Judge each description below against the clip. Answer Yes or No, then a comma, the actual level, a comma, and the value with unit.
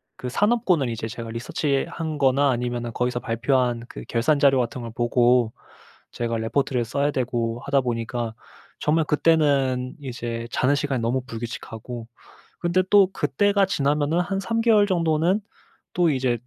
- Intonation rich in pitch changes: No, average, 4.7 semitones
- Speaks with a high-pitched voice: No, low, 130 Hz